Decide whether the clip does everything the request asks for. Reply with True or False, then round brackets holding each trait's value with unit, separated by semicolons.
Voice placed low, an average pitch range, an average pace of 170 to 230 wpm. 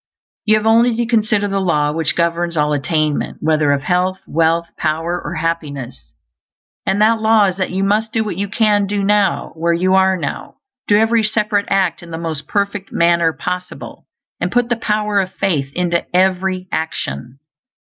False (185 Hz; 4.1 semitones; 180 wpm)